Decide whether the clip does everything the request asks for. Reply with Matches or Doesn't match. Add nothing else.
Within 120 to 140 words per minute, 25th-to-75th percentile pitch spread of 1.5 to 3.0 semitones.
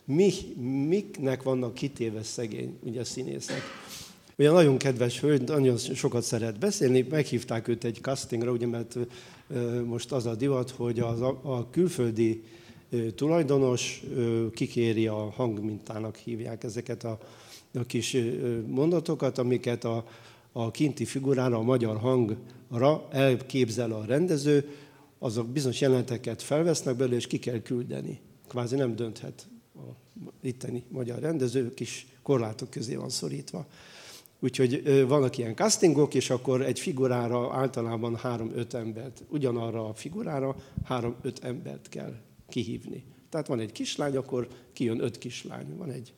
Matches